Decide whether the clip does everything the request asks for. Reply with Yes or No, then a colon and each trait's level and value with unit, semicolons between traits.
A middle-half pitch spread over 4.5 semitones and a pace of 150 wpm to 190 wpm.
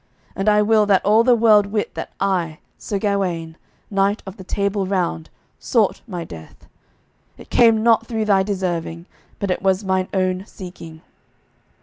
No: narrow, 2.4 semitones; average, 160 wpm